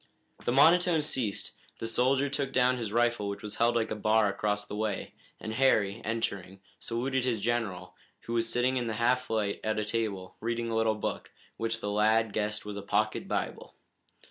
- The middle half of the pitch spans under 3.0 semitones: Yes, narrow, 2.5 semitones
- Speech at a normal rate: Yes, average, 195 wpm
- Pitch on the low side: Yes, low, 115 Hz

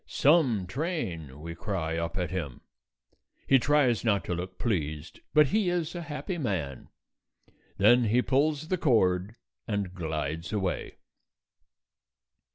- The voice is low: Yes, low, 100 Hz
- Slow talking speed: Yes, slow, 130 wpm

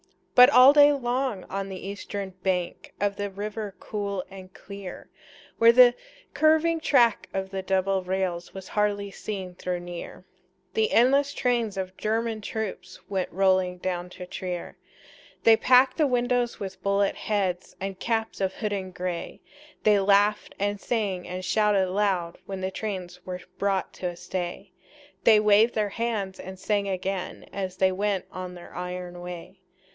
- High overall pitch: Yes, high, 195 Hz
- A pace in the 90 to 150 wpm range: No, average, 160 wpm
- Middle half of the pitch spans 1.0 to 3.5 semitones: Yes, average, 2.9 semitones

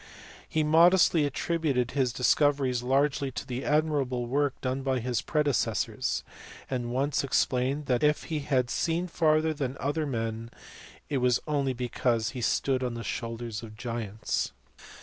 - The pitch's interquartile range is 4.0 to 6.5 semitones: No, average, 3.3 semitones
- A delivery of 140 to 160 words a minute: Yes, average, 150 wpm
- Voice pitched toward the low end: Yes, low, 130 Hz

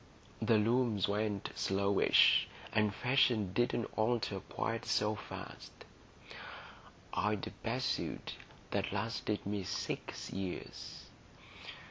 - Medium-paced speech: No, slow, 100 wpm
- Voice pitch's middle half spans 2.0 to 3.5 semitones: Yes, narrow, 2.5 semitones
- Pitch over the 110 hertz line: No, low, 105 Hz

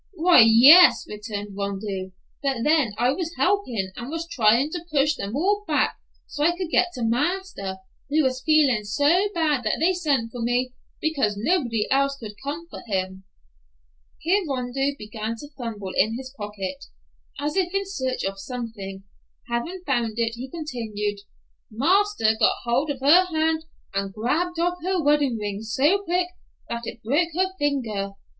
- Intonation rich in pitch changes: Yes, wide, 6.8 semitones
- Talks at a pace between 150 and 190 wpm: Yes, average, 165 wpm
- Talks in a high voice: Yes, very high, 265 Hz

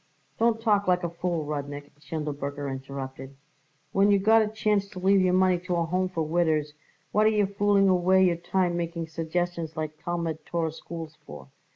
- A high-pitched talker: No, medium, 175 Hz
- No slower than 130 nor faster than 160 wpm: No, average, 185 wpm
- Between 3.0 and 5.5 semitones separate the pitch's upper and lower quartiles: Yes, average, 3.6 semitones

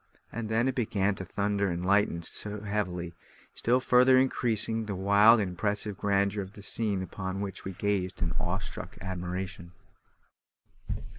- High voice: No, low, 100 Hz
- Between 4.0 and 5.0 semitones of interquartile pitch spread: No, narrow, 2.4 semitones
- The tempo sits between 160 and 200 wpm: No, average, 150 wpm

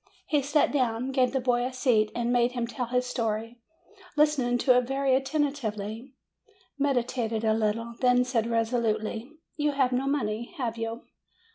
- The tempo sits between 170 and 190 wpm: No, average, 160 wpm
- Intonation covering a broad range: No, average, 2.7 semitones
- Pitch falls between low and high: No, high, 245 Hz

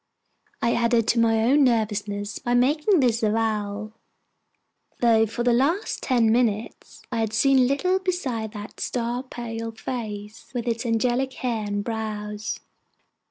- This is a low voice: No, high, 230 Hz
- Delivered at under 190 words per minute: Yes, average, 140 wpm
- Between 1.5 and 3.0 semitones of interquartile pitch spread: Yes, narrow, 2.5 semitones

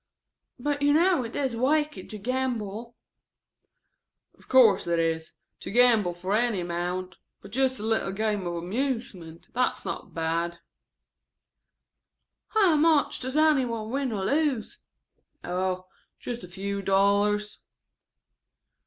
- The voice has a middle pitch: No, high, 220 Hz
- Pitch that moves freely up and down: Yes, wide, 5.9 semitones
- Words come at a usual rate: No, slow, 125 wpm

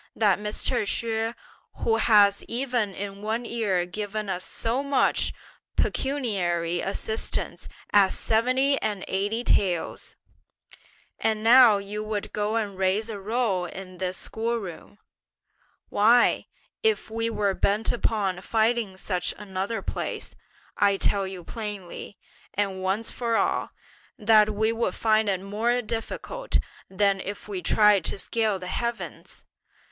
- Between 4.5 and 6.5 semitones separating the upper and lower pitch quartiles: No, average, 2.8 semitones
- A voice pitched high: Yes, high, 210 Hz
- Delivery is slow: Yes, slow, 130 wpm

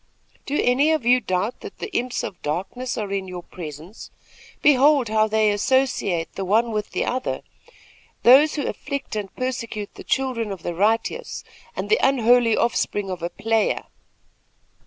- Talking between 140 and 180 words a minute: Yes, average, 160 wpm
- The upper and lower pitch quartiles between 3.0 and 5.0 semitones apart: Yes, average, 4.7 semitones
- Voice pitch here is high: Yes, high, 225 Hz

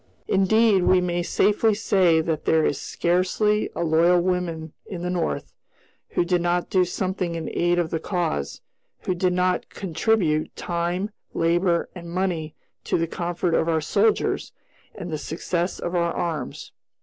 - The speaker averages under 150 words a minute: No, average, 160 wpm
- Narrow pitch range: Yes, narrow, 1.7 semitones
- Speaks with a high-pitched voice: No, medium, 175 Hz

